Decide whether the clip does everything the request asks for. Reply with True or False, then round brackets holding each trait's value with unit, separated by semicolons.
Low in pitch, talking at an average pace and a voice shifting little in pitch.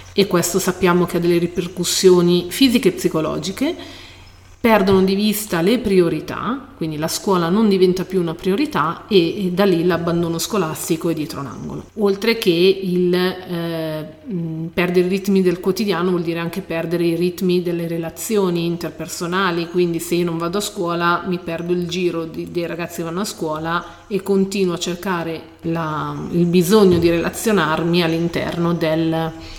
False (175 Hz; 160 wpm; 2.2 semitones)